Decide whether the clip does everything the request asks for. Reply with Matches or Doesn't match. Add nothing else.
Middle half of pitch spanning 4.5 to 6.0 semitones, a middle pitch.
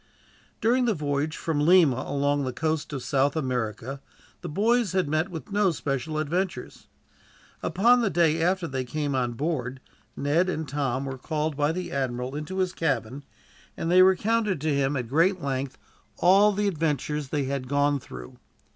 Matches